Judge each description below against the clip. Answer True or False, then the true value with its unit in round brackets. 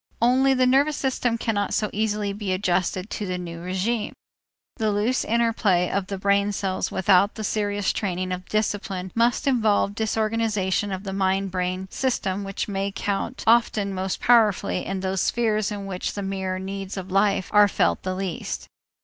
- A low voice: False (200 Hz)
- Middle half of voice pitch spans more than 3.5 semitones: False (2.6 semitones)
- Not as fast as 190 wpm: True (170 wpm)